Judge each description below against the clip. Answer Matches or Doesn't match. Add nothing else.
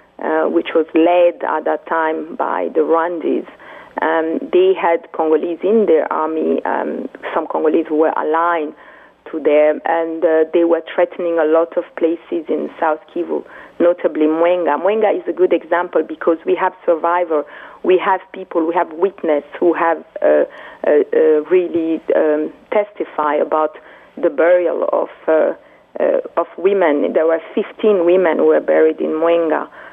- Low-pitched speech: Doesn't match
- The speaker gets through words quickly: Doesn't match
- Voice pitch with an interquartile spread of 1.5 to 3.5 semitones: Matches